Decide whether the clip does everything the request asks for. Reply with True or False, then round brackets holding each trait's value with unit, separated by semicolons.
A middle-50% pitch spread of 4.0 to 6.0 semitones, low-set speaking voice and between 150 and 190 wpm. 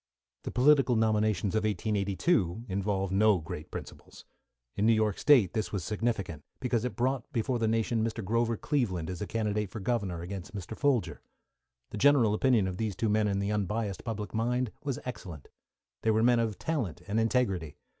False (3.2 semitones; 110 Hz; 180 wpm)